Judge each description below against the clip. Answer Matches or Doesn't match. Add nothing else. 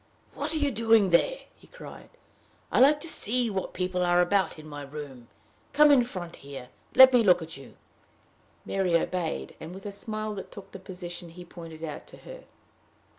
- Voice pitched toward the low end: Doesn't match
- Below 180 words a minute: Doesn't match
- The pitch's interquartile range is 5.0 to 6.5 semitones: Matches